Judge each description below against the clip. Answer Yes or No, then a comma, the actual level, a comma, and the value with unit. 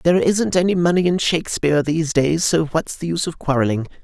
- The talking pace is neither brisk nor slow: No, fast, 210 wpm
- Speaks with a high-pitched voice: No, medium, 165 Hz